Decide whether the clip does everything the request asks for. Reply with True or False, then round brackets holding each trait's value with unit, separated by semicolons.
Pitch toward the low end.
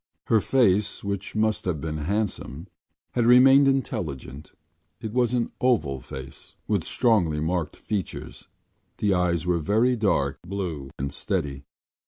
True (95 Hz)